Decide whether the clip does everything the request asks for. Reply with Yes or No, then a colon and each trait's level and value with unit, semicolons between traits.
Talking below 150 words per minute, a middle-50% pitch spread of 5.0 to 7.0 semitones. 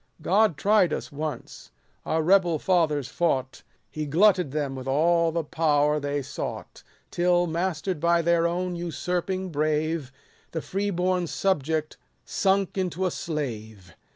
No: slow, 135 wpm; average, 3.2 semitones